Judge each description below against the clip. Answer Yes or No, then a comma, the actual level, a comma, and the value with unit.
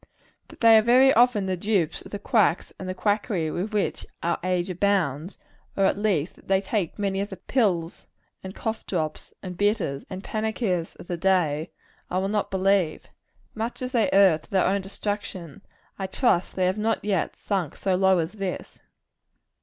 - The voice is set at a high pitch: Yes, high, 195 Hz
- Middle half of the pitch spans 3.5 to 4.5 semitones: No, average, 2.7 semitones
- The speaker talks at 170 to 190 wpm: Yes, average, 185 wpm